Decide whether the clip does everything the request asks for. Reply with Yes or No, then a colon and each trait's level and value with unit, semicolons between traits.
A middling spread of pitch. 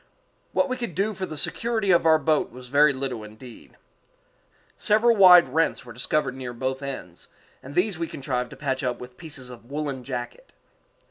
No: wide, 5.8 semitones